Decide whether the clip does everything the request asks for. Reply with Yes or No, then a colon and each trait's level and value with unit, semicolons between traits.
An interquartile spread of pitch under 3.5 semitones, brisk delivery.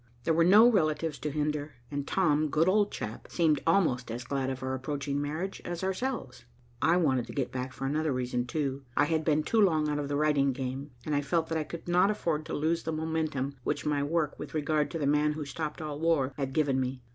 Yes: average, 2.8 semitones; fast, 235 wpm